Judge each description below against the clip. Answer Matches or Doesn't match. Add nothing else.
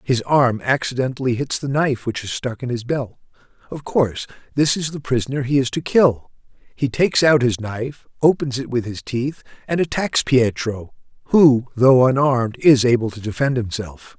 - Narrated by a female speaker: Doesn't match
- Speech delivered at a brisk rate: Doesn't match